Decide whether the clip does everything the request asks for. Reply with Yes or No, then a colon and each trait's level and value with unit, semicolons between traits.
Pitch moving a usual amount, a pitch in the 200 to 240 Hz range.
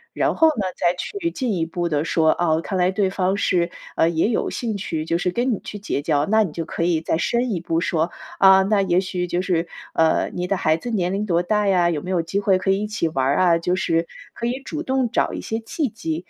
No: average, 4.0 semitones; medium, 185 Hz